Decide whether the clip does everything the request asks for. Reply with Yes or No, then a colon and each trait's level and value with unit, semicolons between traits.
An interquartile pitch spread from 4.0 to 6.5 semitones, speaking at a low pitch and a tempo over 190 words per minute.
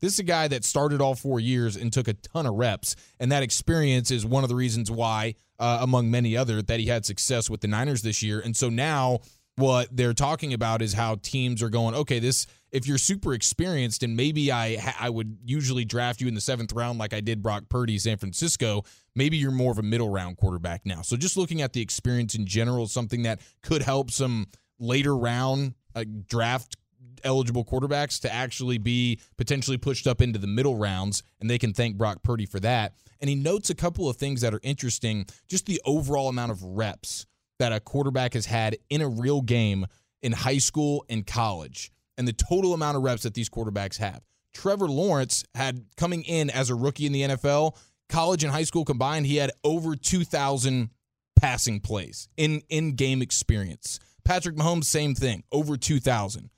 No: average, 3.6 semitones; low, 125 Hz; fast, 205 wpm